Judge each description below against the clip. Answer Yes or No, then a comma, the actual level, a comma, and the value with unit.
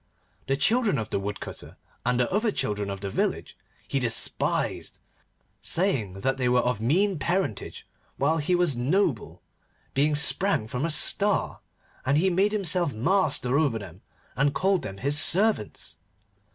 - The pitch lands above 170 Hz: No, medium, 140 Hz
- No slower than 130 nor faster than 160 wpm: Yes, average, 150 wpm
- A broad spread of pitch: Yes, wide, 8.2 semitones